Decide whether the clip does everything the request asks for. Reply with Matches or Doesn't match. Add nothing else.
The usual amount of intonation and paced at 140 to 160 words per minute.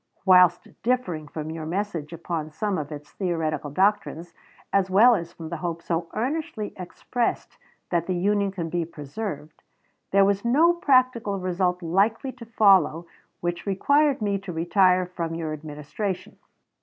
Matches